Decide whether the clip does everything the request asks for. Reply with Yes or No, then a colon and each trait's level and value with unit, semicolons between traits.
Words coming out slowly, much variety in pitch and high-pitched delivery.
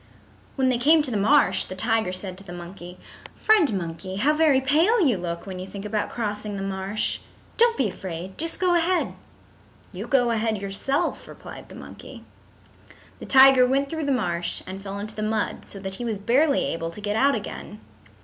No: average, 195 wpm; wide, 6.2 semitones; high, 215 Hz